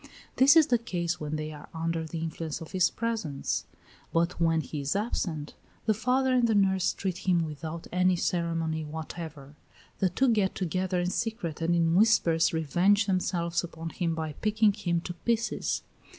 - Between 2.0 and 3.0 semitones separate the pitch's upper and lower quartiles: No, average, 3.9 semitones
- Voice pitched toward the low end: No, medium, 175 Hz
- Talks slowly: No, average, 175 wpm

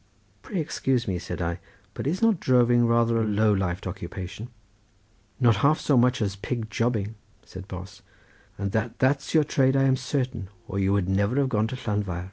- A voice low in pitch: Yes, low, 115 Hz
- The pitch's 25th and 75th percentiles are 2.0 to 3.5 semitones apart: No, average, 4.8 semitones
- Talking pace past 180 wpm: Yes, average, 190 wpm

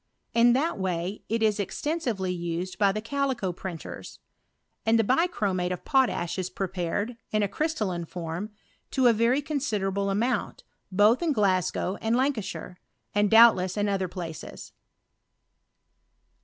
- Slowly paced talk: Yes, slow, 130 wpm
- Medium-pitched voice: No, high, 205 Hz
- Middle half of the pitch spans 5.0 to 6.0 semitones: No, average, 4.6 semitones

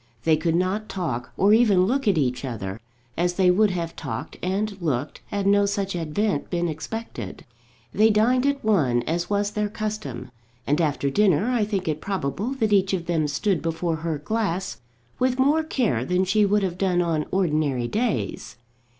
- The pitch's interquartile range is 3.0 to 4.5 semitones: No, average, 5.1 semitones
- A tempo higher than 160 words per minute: Yes, average, 180 wpm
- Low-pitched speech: No, medium, 185 Hz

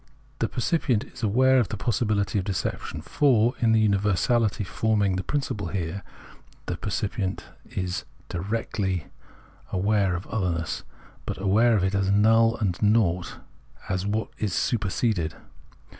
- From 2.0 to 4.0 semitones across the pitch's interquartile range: Yes, average, 3.0 semitones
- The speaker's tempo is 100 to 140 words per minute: Yes, slow, 135 wpm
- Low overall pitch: Yes, low, 105 Hz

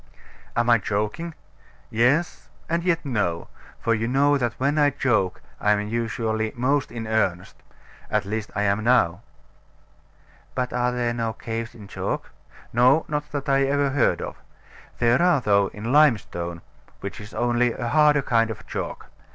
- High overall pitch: No, low, 120 Hz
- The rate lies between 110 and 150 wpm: No, average, 160 wpm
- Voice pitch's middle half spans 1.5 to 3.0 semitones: No, average, 4.3 semitones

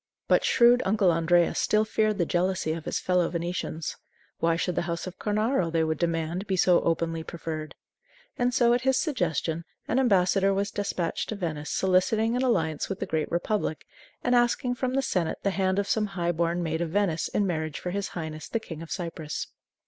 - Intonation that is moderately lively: Yes, average, 4.3 semitones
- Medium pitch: Yes, medium, 180 Hz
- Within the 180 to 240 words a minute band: Yes, average, 200 wpm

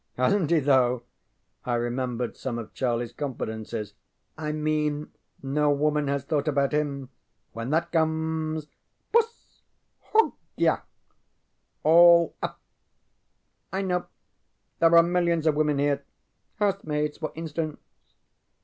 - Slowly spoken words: Yes, slow, 115 wpm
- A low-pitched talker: No, medium, 150 Hz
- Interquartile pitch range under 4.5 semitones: Yes, average, 3.4 semitones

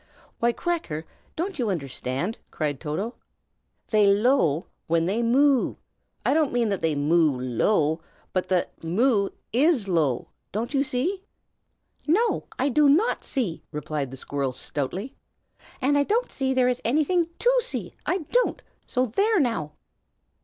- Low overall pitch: No, high, 230 Hz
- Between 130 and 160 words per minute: Yes, average, 145 wpm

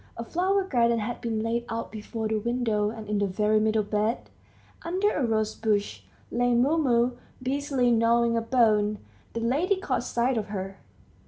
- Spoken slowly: No, average, 165 wpm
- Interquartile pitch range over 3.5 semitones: No, average, 2.7 semitones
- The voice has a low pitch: No, high, 230 Hz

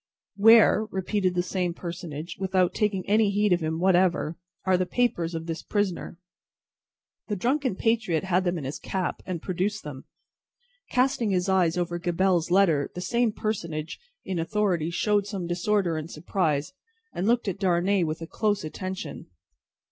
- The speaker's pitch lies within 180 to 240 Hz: Yes, medium, 185 Hz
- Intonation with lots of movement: No, average, 3.2 semitones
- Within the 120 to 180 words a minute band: Yes, average, 160 wpm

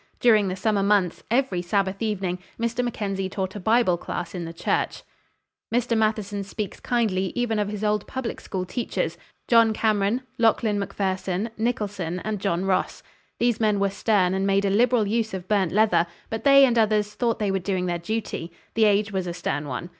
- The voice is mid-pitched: No, high, 205 Hz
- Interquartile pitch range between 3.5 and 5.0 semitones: No, average, 2.9 semitones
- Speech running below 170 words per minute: No, average, 185 wpm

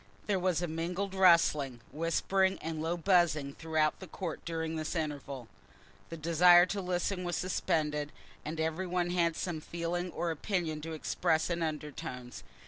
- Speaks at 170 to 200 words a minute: No, average, 155 wpm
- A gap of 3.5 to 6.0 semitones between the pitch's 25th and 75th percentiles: No, narrow, 2.4 semitones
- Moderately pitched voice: Yes, medium, 165 Hz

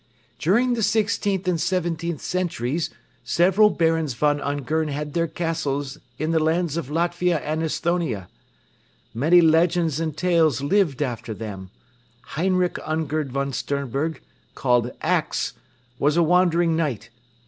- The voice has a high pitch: No, medium, 160 Hz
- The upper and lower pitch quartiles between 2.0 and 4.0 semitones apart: Yes, average, 3.6 semitones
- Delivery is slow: Yes, slow, 125 wpm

